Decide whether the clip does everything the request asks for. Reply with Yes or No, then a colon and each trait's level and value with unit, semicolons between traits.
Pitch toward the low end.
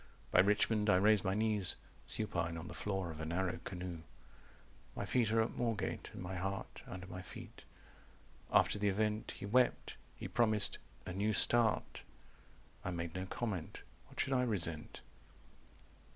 Yes: low, 100 Hz